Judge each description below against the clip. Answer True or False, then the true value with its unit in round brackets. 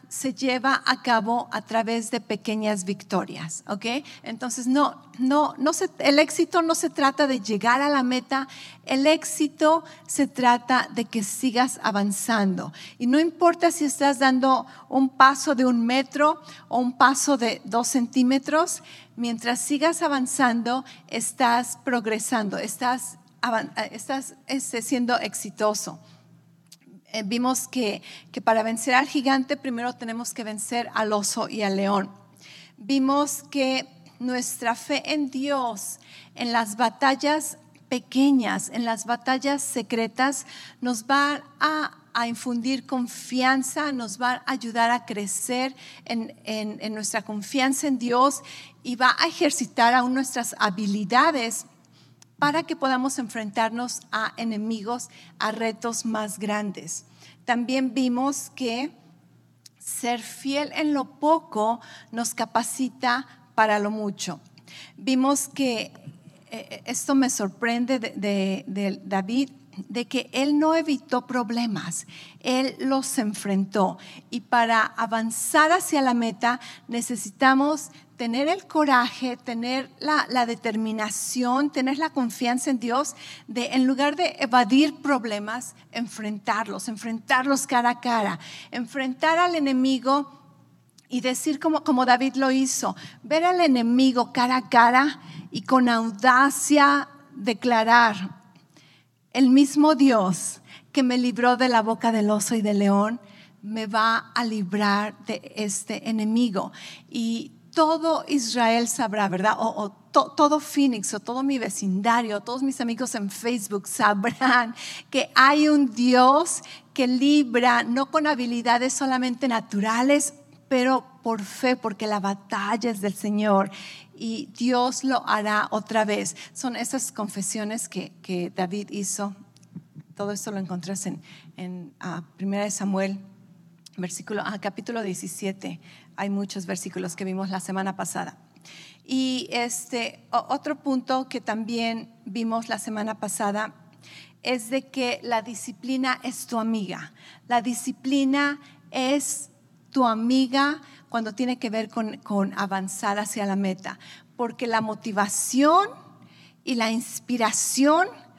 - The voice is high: True (240 Hz)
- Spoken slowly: True (130 wpm)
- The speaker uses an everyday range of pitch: True (3.8 semitones)